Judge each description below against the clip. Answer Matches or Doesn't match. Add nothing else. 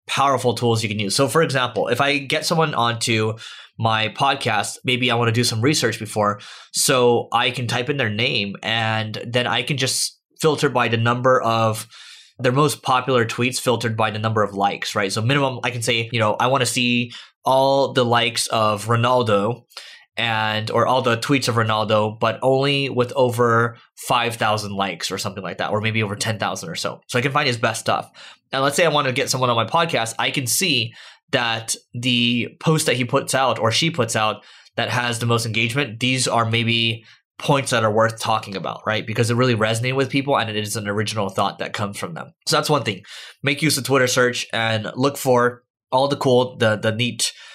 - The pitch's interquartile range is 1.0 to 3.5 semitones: Matches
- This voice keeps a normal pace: Doesn't match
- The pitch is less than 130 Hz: Matches